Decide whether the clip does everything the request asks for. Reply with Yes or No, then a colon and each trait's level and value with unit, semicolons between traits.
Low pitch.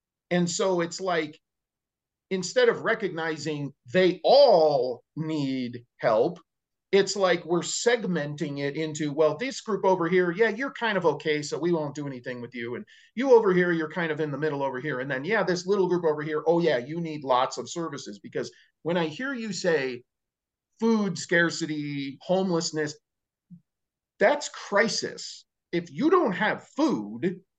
No: medium, 165 Hz